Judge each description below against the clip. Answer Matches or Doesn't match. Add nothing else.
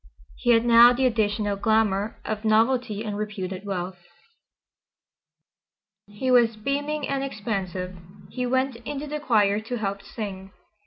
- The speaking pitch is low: Doesn't match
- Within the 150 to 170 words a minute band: Doesn't match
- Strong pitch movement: Doesn't match